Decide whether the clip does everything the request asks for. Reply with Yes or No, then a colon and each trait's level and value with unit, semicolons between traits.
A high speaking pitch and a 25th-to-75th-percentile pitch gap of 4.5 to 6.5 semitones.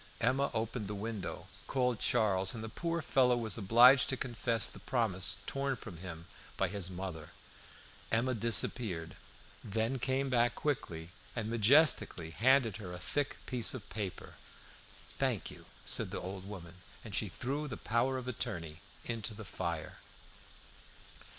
No: low, 115 Hz; average, 5.0 semitones